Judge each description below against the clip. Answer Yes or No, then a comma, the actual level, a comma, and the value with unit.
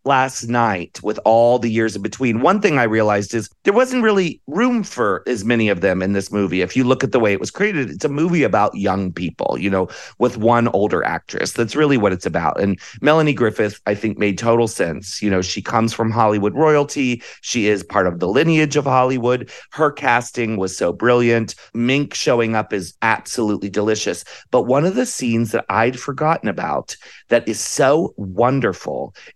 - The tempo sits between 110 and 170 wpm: No, average, 200 wpm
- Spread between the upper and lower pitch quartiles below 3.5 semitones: No, average, 4.4 semitones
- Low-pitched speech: Yes, low, 115 Hz